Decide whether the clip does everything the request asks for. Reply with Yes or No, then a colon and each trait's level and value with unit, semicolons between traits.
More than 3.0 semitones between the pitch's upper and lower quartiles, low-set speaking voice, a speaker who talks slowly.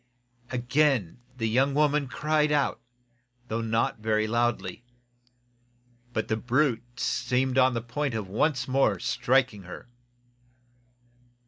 Yes: average, 3.4 semitones; low, 125 Hz; slow, 115 wpm